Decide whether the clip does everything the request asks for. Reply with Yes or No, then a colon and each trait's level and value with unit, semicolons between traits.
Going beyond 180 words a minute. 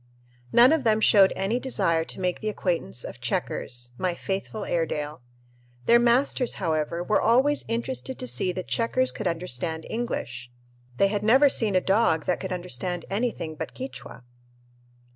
No: average, 160 wpm